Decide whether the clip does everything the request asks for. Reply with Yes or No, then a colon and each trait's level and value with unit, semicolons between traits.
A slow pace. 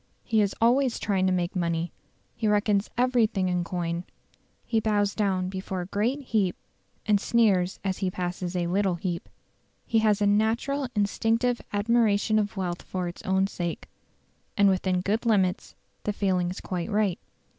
No: average, 165 wpm